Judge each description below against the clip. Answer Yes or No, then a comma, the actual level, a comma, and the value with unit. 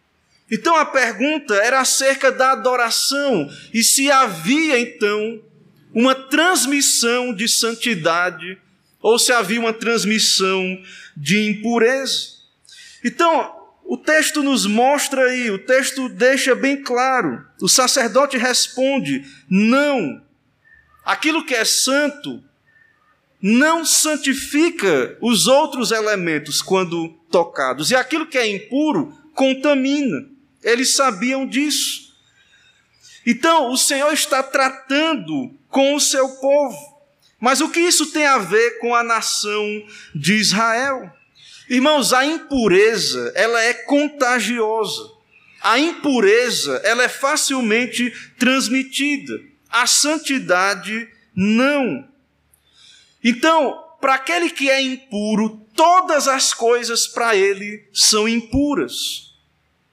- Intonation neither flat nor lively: Yes, average, 4.0 semitones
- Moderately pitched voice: No, very high, 260 Hz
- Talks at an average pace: No, slow, 105 wpm